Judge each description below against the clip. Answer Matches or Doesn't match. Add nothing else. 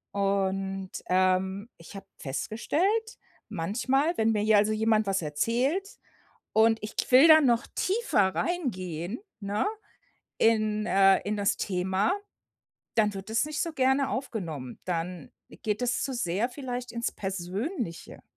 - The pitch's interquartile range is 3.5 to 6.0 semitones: Matches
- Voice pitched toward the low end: Doesn't match